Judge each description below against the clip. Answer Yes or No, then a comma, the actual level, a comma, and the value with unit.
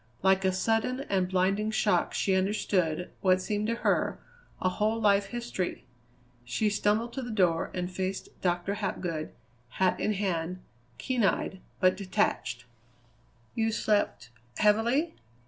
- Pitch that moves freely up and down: No, average, 2.8 semitones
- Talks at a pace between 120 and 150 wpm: Yes, slow, 135 wpm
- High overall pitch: Yes, high, 195 Hz